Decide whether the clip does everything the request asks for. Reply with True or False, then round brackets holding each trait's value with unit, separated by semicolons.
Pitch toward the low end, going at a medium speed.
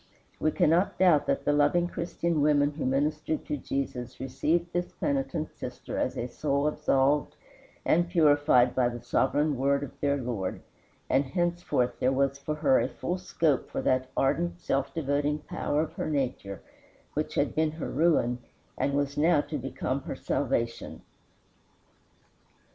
False (145 Hz; 155 wpm)